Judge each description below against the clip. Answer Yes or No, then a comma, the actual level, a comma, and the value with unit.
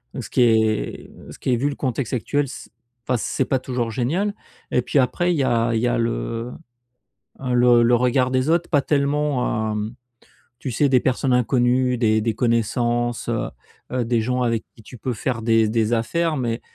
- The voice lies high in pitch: No, low, 125 Hz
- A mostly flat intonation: Yes, narrow, 2.2 semitones